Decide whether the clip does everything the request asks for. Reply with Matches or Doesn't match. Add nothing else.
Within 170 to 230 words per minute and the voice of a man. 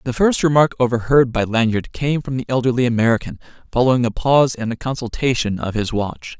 Matches